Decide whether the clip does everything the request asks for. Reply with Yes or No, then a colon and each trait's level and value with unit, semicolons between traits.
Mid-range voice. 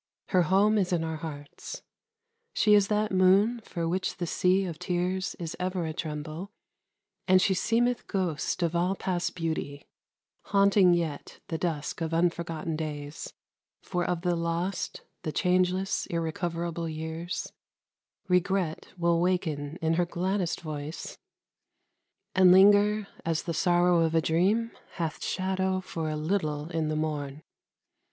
Yes: medium, 175 Hz